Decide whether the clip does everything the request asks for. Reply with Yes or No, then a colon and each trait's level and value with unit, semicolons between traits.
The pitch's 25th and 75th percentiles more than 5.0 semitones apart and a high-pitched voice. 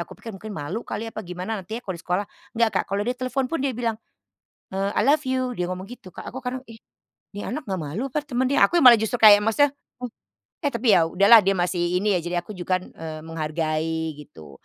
Yes: wide, 5.6 semitones; high, 205 Hz